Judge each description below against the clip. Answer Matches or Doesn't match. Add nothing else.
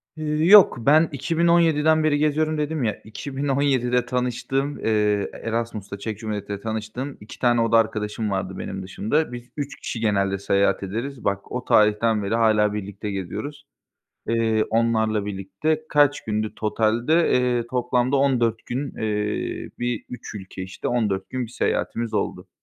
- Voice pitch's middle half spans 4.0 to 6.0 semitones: Matches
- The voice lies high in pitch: Doesn't match